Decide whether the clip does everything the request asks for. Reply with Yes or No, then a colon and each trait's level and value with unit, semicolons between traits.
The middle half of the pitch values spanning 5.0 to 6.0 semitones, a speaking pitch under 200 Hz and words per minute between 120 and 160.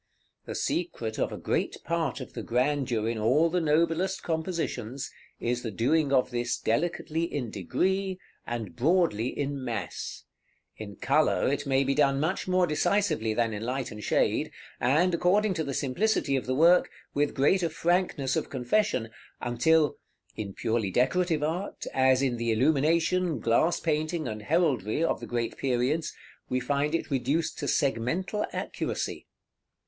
Yes: wide, 5.6 semitones; medium, 140 Hz; average, 155 wpm